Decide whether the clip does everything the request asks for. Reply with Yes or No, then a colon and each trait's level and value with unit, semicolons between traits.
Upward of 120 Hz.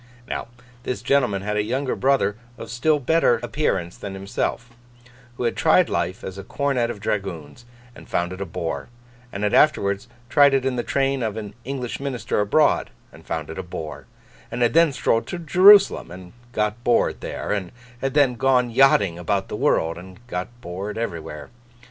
No: low, 115 Hz